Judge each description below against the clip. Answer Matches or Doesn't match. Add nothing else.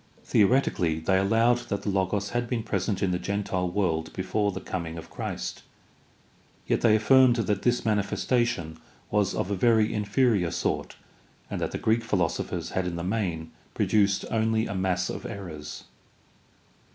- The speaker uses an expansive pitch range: Doesn't match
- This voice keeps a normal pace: Matches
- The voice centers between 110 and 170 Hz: Doesn't match